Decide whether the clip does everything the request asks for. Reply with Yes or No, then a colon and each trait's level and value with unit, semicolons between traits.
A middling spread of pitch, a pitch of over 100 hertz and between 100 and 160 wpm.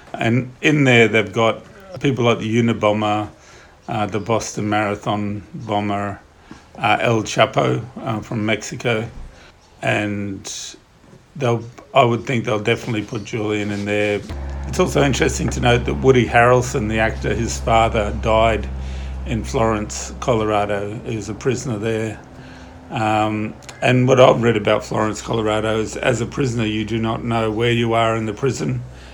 No: narrow, 2.2 semitones; low, 110 Hz; average, 150 wpm